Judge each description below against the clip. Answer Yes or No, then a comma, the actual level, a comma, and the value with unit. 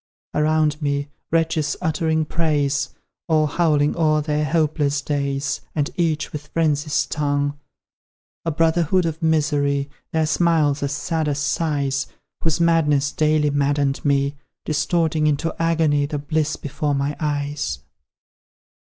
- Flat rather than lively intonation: Yes, narrow, 1.8 semitones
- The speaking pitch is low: No, medium, 150 Hz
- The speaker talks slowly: Yes, slow, 125 wpm